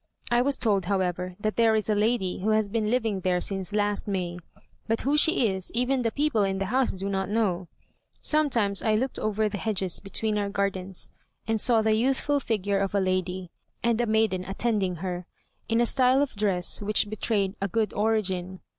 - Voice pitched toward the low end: No, high, 210 Hz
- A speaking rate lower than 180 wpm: No, average, 200 wpm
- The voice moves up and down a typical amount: Yes, average, 3.0 semitones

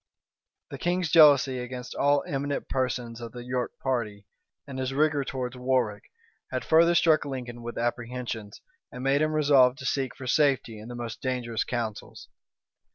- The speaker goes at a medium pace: Yes, average, 160 wpm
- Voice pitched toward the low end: Yes, low, 130 Hz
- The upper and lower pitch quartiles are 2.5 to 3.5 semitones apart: Yes, average, 2.8 semitones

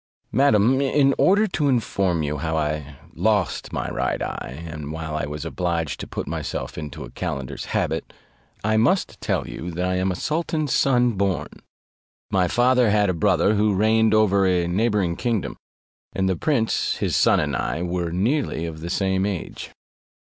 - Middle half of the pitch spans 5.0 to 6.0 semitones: Yes, average, 5.3 semitones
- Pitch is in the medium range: No, very low, 95 Hz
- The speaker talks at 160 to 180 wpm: Yes, average, 175 wpm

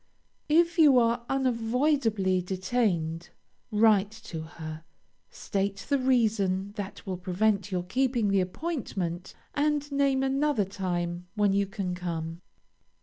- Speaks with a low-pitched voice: No, high, 205 Hz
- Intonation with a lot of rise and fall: Yes, wide, 5.9 semitones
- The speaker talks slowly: Yes, slow, 120 wpm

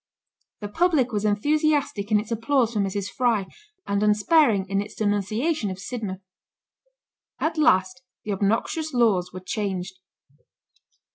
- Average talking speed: No, slow, 130 wpm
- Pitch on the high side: Yes, high, 210 Hz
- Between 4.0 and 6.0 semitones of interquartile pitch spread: Yes, average, 4.4 semitones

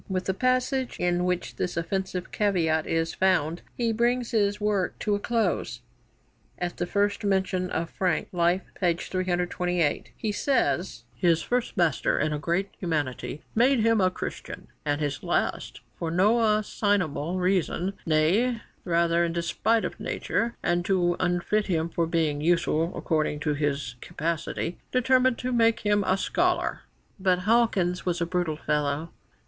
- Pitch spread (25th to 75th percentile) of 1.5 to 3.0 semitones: No, average, 3.8 semitones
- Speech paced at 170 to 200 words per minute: No, average, 155 wpm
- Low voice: No, medium, 180 Hz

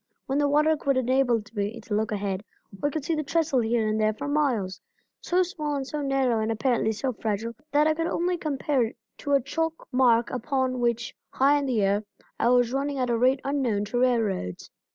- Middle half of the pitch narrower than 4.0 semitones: No, average, 4.3 semitones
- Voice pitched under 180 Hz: No, very high, 255 Hz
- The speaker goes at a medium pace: No, fast, 215 wpm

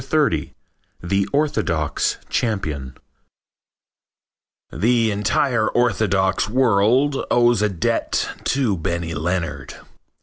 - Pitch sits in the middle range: No, low, 100 Hz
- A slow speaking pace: Yes, slow, 80 wpm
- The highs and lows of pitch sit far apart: Yes, wide, 5.9 semitones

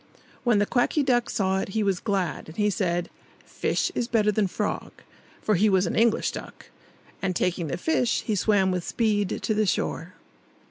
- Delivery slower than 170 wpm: No, average, 190 wpm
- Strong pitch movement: No, average, 3.0 semitones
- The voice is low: No, high, 205 Hz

